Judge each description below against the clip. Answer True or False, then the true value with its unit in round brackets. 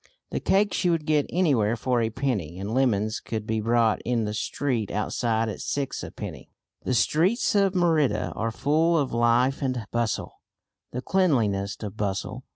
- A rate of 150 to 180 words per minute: True (170 wpm)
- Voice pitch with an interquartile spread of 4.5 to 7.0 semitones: True (5.4 semitones)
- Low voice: True (120 Hz)